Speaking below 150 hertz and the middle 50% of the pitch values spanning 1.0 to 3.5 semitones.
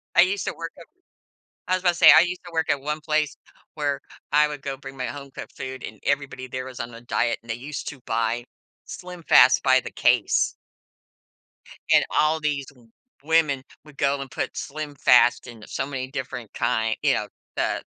Yes: medium, 140 Hz; average, 3.0 semitones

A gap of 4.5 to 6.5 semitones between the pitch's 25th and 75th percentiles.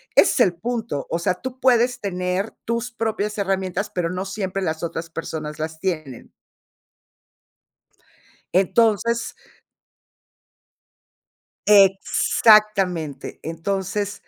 No: average, 4.1 semitones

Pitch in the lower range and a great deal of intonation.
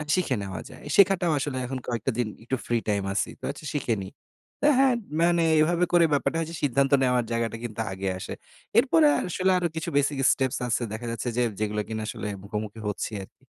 Yes: low, 130 Hz; wide, 6.6 semitones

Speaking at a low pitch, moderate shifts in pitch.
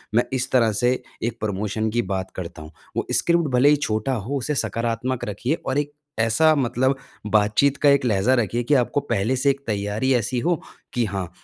Yes: low, 120 Hz; average, 4.2 semitones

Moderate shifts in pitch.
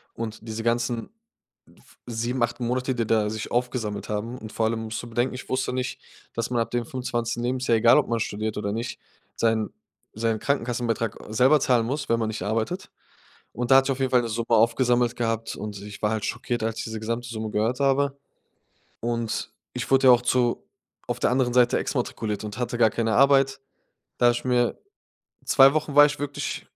No: narrow, 2.1 semitones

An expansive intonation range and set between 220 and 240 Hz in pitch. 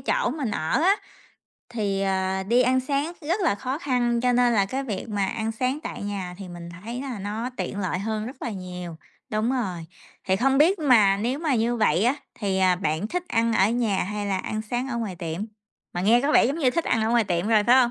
No: average, 4.5 semitones; high, 225 Hz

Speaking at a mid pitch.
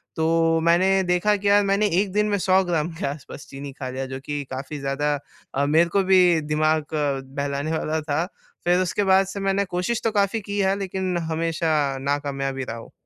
Yes: medium, 165 Hz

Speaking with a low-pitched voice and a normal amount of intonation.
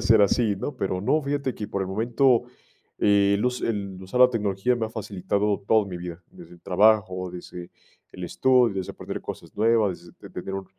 Yes: low, 100 Hz; average, 3.6 semitones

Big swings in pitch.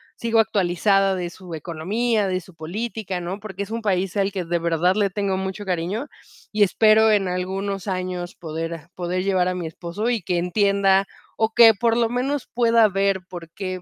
No: average, 3.2 semitones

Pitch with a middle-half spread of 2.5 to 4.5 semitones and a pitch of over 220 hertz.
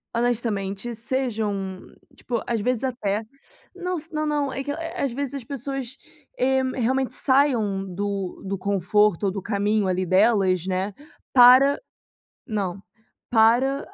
No: average, 5.0 semitones; high, 230 Hz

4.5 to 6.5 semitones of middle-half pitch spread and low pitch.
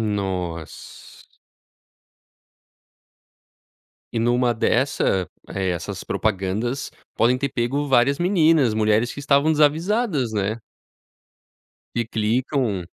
Yes: average, 5.3 semitones; low, 120 Hz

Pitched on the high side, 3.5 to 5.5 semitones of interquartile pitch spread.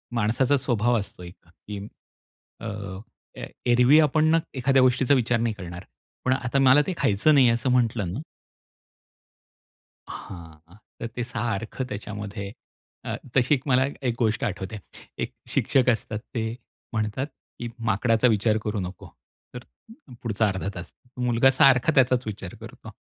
No: low, 115 Hz; average, 3.9 semitones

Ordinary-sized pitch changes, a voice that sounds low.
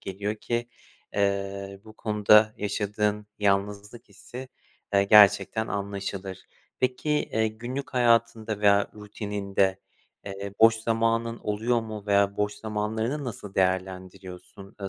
No: narrow, 2.1 semitones; low, 105 Hz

